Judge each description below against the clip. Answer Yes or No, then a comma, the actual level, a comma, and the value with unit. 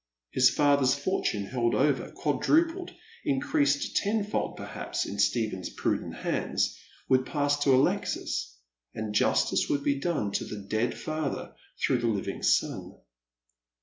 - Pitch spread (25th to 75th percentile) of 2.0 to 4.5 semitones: No, average, 4.9 semitones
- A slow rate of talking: Yes, slow, 130 wpm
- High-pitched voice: No, low, 135 Hz